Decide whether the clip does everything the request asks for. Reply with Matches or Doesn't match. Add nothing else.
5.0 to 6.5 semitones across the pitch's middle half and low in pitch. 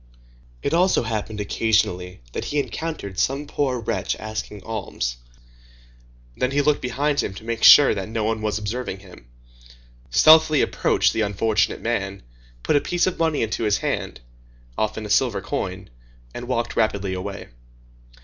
Matches